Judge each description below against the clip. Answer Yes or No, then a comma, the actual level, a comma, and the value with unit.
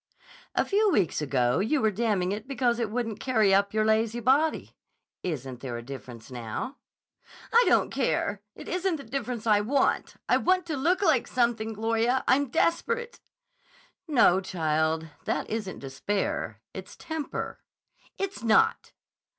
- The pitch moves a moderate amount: No, wide, 6.8 semitones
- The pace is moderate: Yes, average, 150 wpm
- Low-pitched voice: No, high, 225 Hz